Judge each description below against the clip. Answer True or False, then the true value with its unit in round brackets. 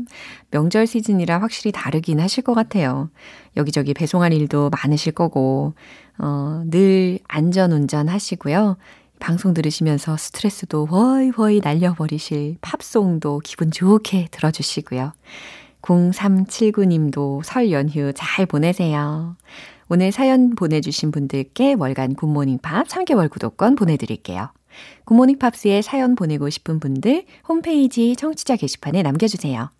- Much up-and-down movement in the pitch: True (6.9 semitones)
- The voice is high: False (175 Hz)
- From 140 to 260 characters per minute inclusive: False (290 characters per minute)